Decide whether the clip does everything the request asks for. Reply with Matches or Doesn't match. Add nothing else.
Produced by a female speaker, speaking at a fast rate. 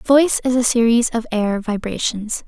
Doesn't match